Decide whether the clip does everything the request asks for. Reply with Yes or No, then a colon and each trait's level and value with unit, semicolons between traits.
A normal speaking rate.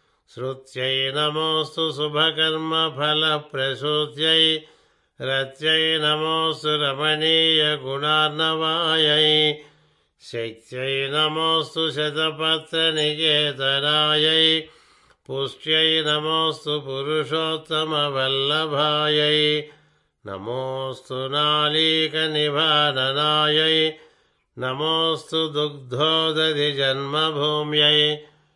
No: slow, 35 wpm